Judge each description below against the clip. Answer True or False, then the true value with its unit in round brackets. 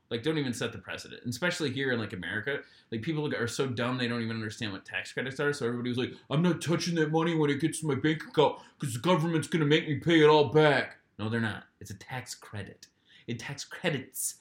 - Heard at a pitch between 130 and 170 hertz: True (140 Hz)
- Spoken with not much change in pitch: False (5.0 semitones)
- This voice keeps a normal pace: False (255 wpm)